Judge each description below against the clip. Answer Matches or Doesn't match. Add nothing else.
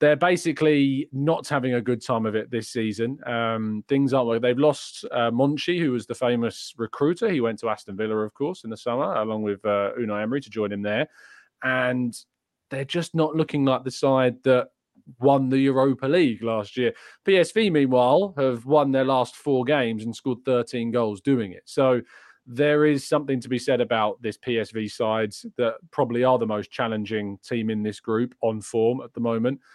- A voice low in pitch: Matches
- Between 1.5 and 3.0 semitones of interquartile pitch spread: Doesn't match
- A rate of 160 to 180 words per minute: Doesn't match